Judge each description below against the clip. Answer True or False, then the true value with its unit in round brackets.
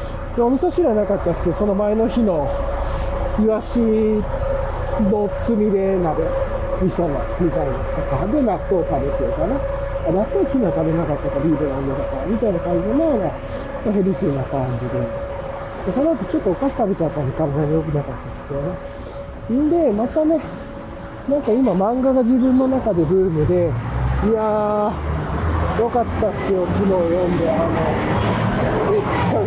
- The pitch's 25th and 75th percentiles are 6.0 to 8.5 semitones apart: True (7.0 semitones)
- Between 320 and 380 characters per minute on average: True (325 characters per minute)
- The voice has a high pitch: True (200 Hz)